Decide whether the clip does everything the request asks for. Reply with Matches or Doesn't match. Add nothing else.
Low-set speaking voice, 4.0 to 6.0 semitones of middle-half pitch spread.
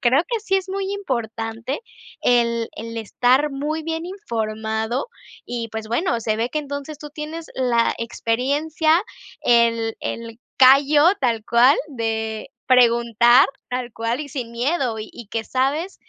Doesn't match